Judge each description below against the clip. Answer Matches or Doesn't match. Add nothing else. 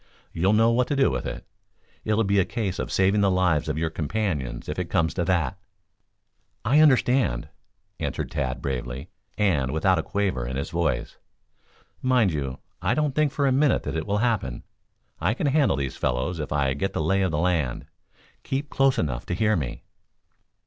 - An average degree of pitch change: Doesn't match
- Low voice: Matches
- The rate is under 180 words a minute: Doesn't match